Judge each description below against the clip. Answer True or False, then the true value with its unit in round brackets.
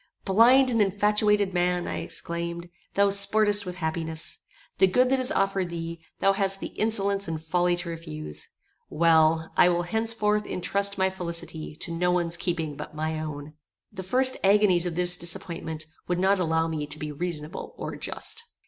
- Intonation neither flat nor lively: True (3.4 semitones)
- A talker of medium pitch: True (180 Hz)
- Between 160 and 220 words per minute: True (170 wpm)